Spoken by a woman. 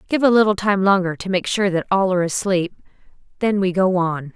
Yes: female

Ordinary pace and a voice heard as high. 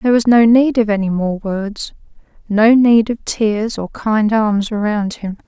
Yes: average, 185 wpm; high, 215 Hz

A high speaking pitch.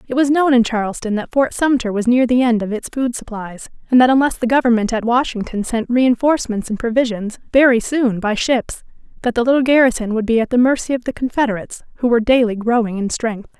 Yes: high, 240 Hz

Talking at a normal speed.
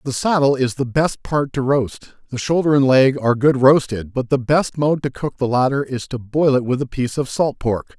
No: fast, 240 wpm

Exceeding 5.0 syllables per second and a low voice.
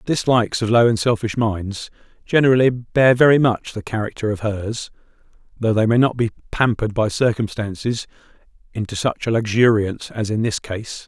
Yes: 5.3 syllables/s; low, 110 Hz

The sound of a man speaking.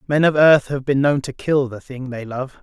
Yes: male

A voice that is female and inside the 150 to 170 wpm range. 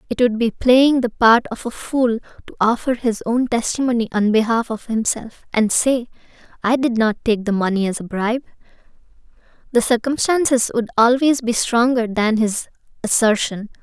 Yes: female; average, 165 wpm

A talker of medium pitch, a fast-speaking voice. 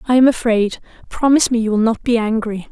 No: high, 230 Hz; fast, 220 wpm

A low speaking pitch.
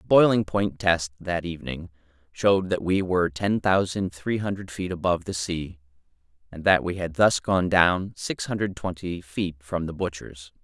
Yes: very low, 90 Hz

